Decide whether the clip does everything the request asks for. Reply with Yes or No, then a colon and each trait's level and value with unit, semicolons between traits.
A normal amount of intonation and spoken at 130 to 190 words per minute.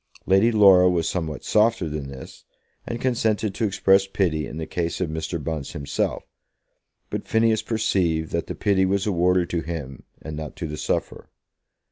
Yes: average, 4.0 semitones; average, 170 wpm